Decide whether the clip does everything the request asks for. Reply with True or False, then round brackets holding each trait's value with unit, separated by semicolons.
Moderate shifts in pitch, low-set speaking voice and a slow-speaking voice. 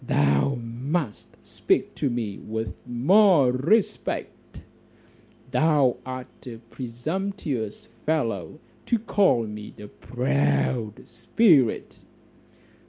False (5.8 semitones; 120 Hz; 90 wpm)